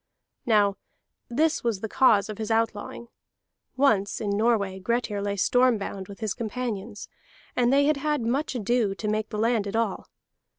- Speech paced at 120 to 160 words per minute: No, average, 170 wpm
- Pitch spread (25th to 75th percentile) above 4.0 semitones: No, average, 3.2 semitones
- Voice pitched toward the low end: No, high, 225 Hz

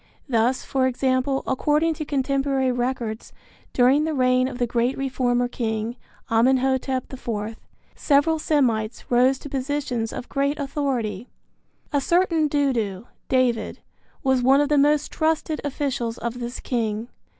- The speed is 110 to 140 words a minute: Yes, slow, 135 wpm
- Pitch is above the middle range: Yes, very high, 260 Hz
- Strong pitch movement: No, average, 2.9 semitones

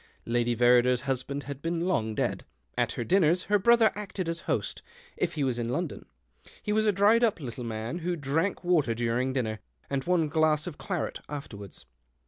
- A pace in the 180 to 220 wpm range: Yes, average, 185 wpm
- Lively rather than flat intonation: Yes, wide, 6.8 semitones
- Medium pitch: Yes, medium, 150 Hz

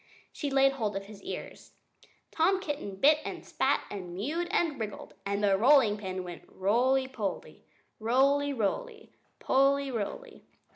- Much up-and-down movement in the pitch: Yes, wide, 5.9 semitones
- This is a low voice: No, very high, 260 Hz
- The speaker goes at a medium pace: Yes, average, 145 wpm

